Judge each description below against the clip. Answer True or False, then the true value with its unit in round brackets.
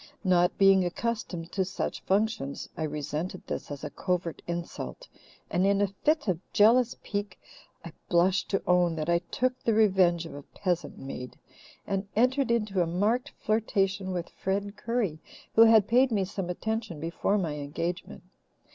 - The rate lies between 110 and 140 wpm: False (165 wpm)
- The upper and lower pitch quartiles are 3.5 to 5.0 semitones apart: True (4.0 semitones)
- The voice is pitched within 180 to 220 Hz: True (190 Hz)